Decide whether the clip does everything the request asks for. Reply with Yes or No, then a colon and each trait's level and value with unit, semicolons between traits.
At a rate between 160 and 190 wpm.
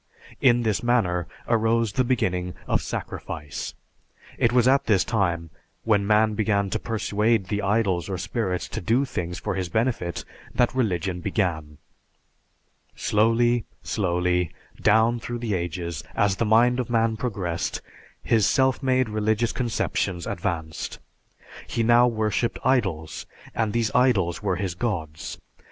No: average, 140 wpm